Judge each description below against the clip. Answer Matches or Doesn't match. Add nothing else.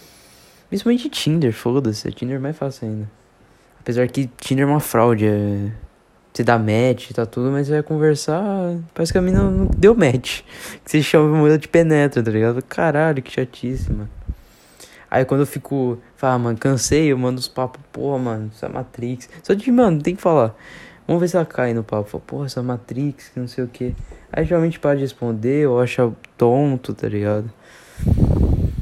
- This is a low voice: Matches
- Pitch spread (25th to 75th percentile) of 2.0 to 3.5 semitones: Doesn't match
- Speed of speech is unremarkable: Doesn't match